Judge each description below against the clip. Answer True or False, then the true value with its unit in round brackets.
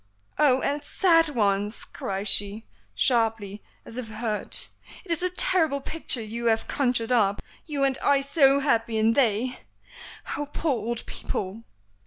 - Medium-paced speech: True (150 wpm)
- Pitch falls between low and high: False (240 Hz)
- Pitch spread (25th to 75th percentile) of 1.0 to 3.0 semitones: False (4.4 semitones)